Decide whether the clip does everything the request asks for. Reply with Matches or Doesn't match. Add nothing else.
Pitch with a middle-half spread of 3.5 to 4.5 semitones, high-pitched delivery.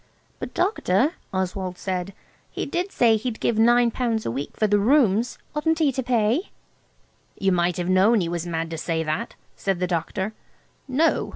Doesn't match